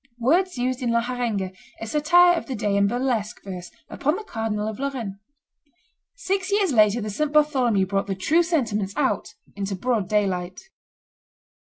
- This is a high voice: Yes, high, 235 Hz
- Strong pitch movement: Yes, wide, 6.7 semitones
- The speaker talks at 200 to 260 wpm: No, average, 165 wpm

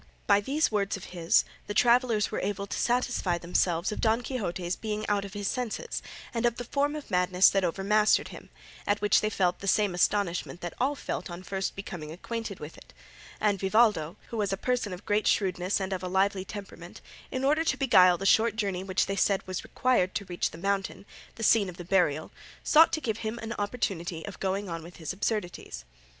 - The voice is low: No, high, 200 Hz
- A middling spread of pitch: Yes, average, 3.4 semitones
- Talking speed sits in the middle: No, fast, 210 wpm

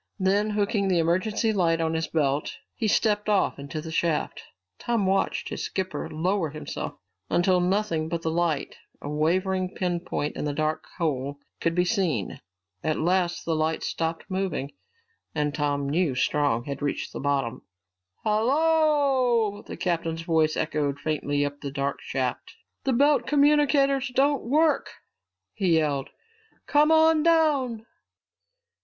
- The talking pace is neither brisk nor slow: Yes, average, 145 wpm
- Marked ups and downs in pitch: Yes, wide, 6.1 semitones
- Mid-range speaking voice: Yes, medium, 175 Hz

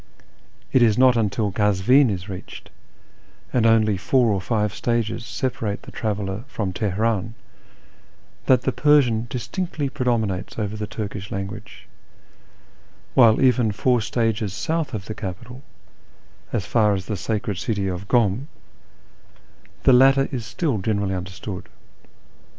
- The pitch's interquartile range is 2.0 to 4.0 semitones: Yes, average, 3.7 semitones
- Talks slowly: Yes, slow, 130 wpm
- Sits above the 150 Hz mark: No, low, 110 Hz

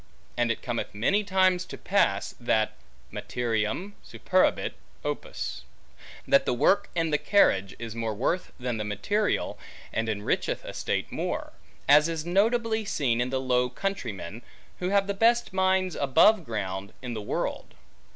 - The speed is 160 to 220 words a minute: No, average, 150 wpm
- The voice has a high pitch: No, low, 135 Hz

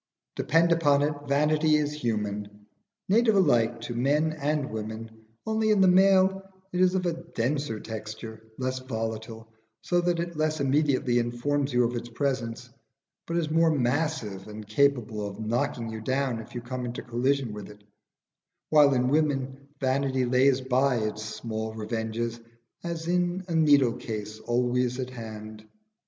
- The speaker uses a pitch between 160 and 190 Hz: No, low, 130 Hz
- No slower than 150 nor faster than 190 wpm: Yes, average, 155 wpm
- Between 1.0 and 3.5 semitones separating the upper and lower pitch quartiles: No, average, 5.1 semitones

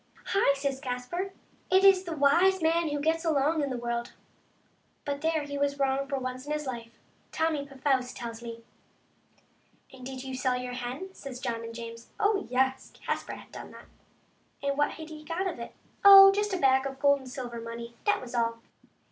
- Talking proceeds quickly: Yes, fast, 215 wpm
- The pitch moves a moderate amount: Yes, average, 4.2 semitones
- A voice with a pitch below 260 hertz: No, very high, 275 Hz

